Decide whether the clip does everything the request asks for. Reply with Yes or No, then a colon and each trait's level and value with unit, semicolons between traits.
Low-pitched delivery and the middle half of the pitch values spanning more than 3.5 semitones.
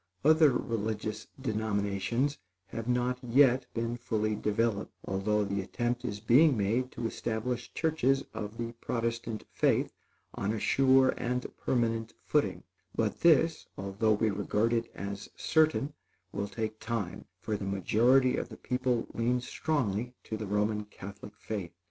No: low, 115 Hz; average, 3.2 semitones